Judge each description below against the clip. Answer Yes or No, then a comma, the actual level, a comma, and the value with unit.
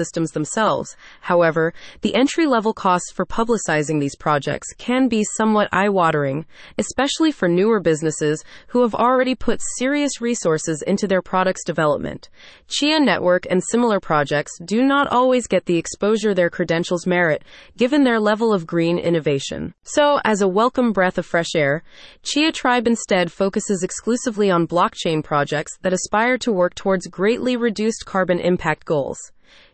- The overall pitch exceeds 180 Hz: Yes, high, 190 Hz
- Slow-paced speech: No, average, 155 wpm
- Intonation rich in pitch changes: Yes, wide, 5.7 semitones